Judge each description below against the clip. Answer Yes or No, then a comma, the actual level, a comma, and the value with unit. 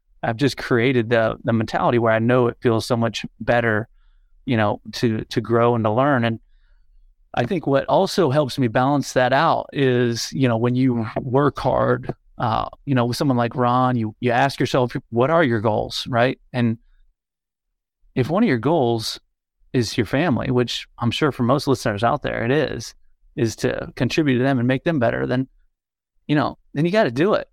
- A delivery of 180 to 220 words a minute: Yes, average, 200 wpm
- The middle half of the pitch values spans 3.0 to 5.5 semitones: No, narrow, 2.6 semitones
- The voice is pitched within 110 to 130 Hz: Yes, low, 120 Hz